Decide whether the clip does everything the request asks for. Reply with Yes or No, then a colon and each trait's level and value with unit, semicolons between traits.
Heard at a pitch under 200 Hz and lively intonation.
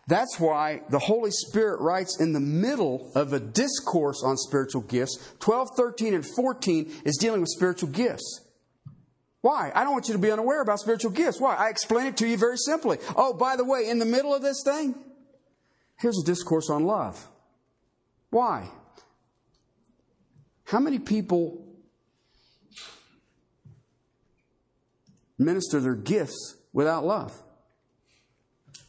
No: high, 205 Hz; wide, 8.7 semitones